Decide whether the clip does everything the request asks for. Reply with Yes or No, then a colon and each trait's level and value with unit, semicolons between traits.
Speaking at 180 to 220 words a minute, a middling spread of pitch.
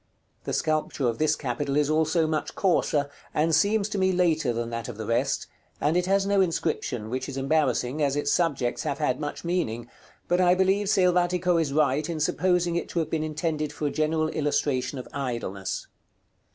Yes: average, 190 wpm; average, 4.3 semitones